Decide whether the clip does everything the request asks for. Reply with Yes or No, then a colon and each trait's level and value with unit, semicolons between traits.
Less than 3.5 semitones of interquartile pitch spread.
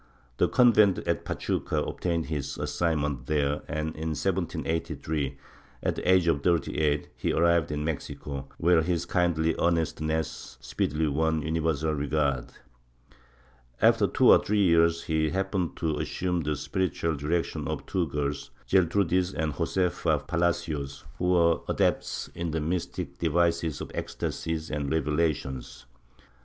Yes: narrow, 2.4 semitones